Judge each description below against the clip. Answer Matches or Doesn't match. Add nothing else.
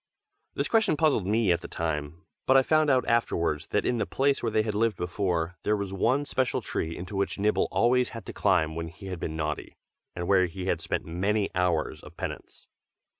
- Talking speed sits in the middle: Doesn't match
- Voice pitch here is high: Doesn't match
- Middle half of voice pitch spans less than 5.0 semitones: Doesn't match